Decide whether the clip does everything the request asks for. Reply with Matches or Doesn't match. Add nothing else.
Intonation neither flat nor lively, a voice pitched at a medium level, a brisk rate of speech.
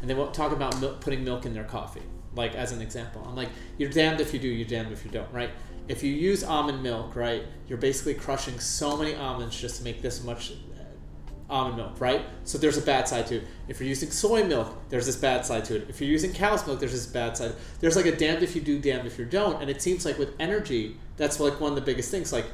Doesn't match